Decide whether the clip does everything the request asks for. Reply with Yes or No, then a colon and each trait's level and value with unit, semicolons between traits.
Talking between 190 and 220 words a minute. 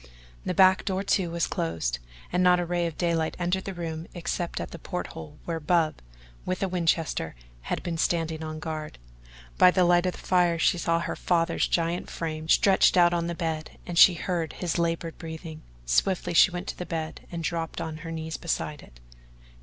Yes: average, 200 wpm